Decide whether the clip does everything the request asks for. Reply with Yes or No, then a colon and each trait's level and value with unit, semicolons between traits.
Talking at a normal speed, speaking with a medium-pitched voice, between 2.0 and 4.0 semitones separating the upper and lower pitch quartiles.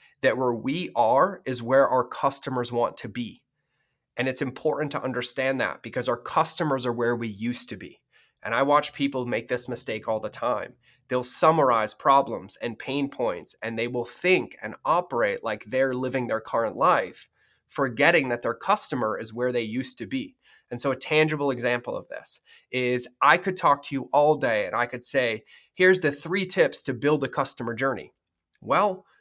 No: average, 190 wpm; low, 130 Hz; average, 2.9 semitones